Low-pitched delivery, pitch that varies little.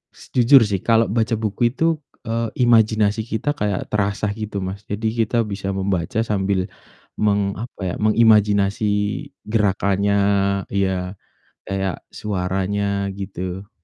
Yes: low, 100 Hz; narrow, 2.2 semitones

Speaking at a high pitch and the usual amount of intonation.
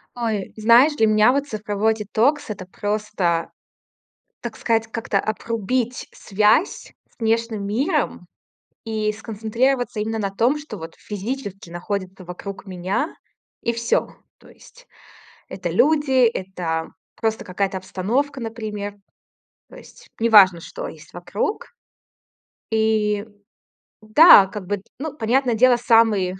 Yes: high, 220 Hz; average, 3.2 semitones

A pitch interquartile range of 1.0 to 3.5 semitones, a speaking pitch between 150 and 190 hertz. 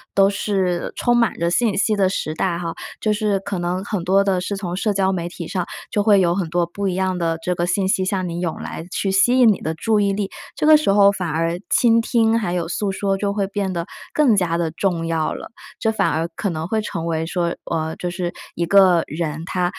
Yes: average, 2.9 semitones; medium, 185 Hz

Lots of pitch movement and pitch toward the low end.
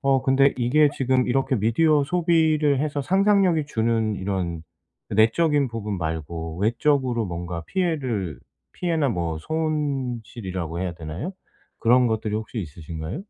Yes: wide, 8.0 semitones; low, 120 Hz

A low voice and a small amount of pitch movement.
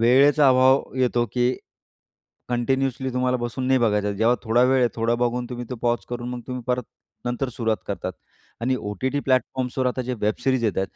Yes: low, 125 Hz; narrow, 1.6 semitones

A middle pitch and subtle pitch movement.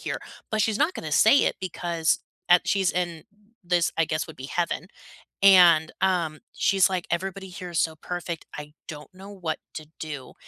No: medium, 175 Hz; average, 3.0 semitones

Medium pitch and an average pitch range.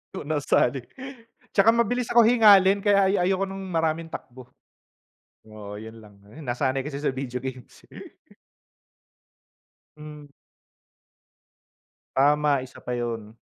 No: medium, 145 Hz; wide, 7.7 semitones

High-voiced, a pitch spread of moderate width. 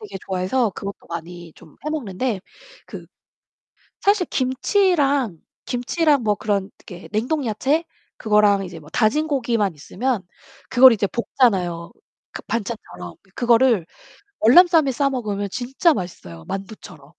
No: high, 225 Hz; wide, 6.0 semitones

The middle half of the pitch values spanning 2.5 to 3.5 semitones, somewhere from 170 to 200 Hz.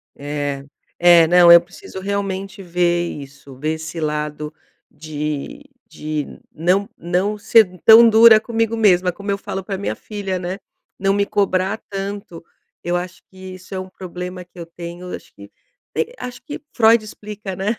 Yes: average, 3.0 semitones; medium, 185 Hz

